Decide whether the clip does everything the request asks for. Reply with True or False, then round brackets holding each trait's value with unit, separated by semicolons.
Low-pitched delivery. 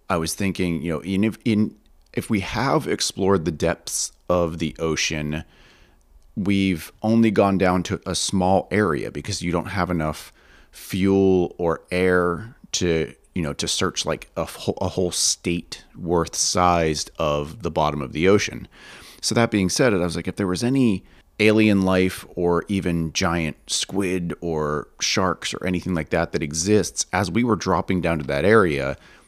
True (90 Hz)